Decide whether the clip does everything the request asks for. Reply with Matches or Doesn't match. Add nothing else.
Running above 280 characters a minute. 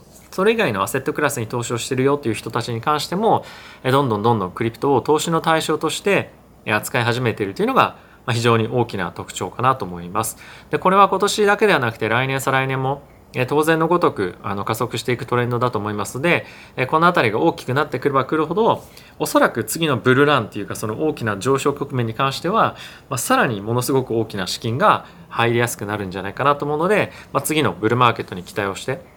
Matches